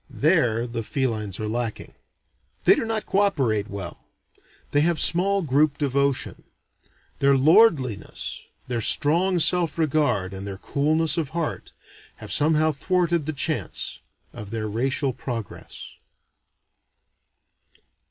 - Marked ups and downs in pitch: Yes, wide, 6.0 semitones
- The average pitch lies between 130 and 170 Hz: Yes, medium, 140 Hz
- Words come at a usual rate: No, slow, 120 wpm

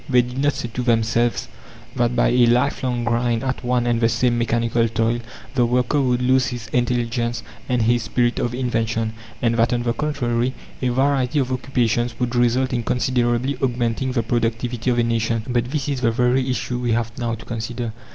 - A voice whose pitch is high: No, low, 120 Hz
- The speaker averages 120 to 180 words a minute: No, average, 195 wpm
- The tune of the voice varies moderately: No, narrow, 1.3 semitones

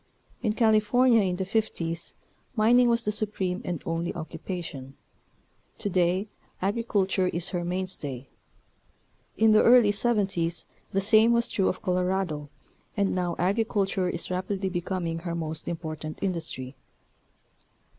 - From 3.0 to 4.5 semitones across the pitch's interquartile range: Yes, average, 3.7 semitones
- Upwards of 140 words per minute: No, slow, 135 wpm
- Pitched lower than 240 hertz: Yes, medium, 185 Hz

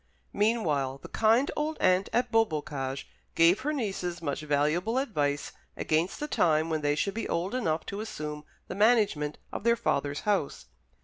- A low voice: No, medium, 175 Hz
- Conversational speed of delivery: Yes, average, 165 wpm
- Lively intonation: Yes, wide, 7.0 semitones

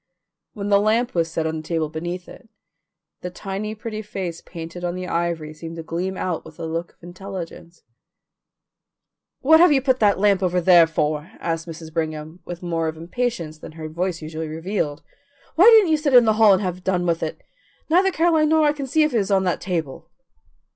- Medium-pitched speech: Yes, medium, 180 Hz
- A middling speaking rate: No, fast, 210 wpm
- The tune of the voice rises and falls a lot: No, average, 4.7 semitones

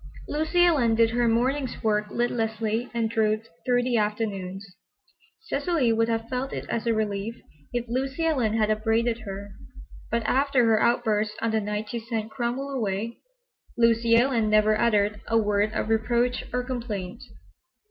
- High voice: Yes, high, 230 Hz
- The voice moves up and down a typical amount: No, narrow, 2.2 semitones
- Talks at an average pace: Yes, average, 160 wpm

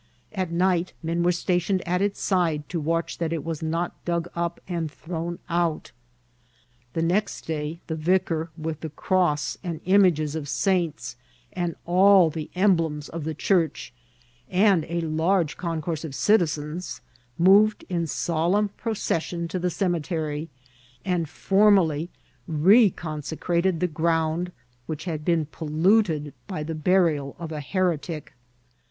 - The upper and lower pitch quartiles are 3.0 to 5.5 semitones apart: No, narrow, 2.5 semitones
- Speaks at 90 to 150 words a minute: Yes, average, 140 wpm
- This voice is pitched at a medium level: Yes, medium, 170 Hz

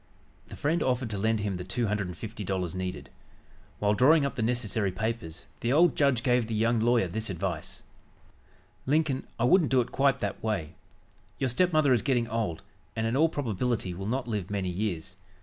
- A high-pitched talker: No, low, 115 Hz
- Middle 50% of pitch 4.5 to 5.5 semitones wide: Yes, average, 4.8 semitones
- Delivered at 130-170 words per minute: No, average, 195 wpm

